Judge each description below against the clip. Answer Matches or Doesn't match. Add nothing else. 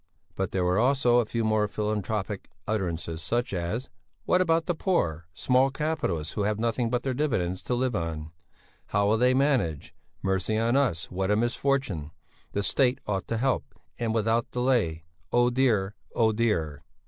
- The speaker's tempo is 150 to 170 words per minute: Matches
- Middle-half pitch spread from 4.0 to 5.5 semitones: Matches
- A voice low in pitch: Matches